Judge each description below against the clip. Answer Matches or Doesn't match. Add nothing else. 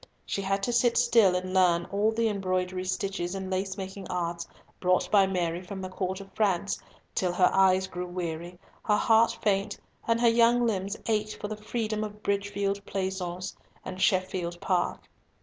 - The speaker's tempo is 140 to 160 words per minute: Doesn't match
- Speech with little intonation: Matches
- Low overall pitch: Doesn't match